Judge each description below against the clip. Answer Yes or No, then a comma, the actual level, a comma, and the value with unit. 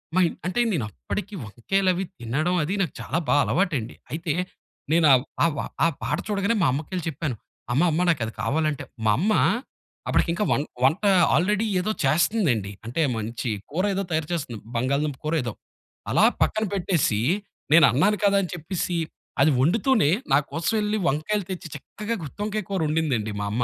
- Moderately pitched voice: Yes, medium, 160 Hz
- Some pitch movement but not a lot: No, wide, 6.1 semitones